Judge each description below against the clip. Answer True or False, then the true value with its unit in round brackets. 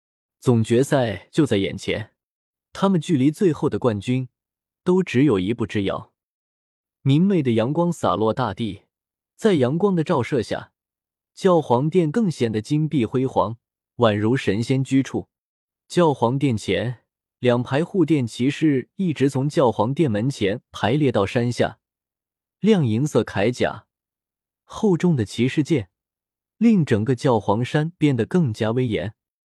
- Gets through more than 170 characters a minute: True (205 characters per minute)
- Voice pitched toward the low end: True (130 Hz)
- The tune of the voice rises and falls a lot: True (6.1 semitones)